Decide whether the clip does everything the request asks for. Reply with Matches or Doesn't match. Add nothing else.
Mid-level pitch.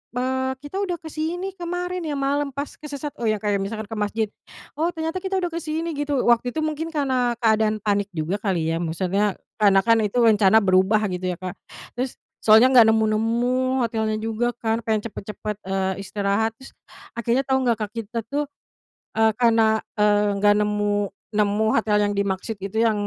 Doesn't match